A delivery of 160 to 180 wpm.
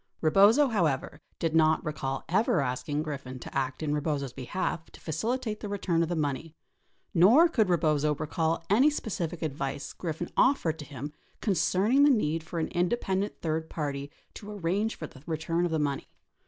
Yes: average, 170 wpm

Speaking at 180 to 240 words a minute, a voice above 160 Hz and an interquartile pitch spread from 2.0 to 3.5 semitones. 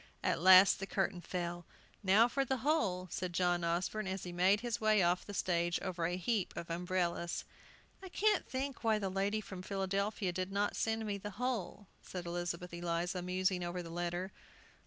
Yes: average, 185 wpm; medium, 185 Hz; average, 3.1 semitones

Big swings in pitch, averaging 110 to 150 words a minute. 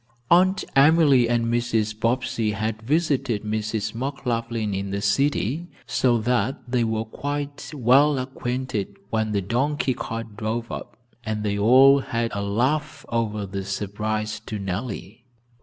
No: average, 3.7 semitones; average, 140 wpm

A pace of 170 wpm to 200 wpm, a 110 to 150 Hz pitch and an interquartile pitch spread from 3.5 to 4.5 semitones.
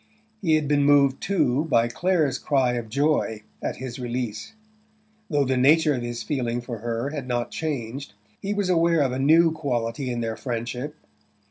Yes: average, 175 wpm; low, 135 Hz; average, 4.2 semitones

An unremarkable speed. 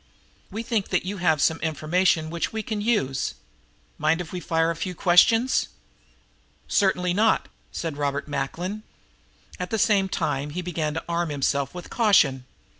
Yes: average, 160 wpm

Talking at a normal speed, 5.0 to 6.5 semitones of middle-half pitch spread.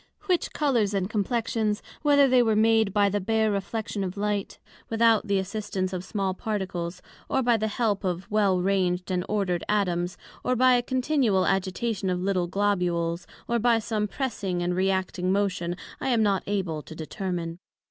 No: average, 175 wpm; average, 3.3 semitones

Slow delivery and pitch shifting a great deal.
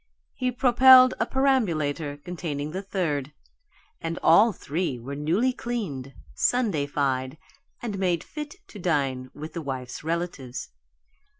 Yes: slow, 120 wpm; wide, 7.6 semitones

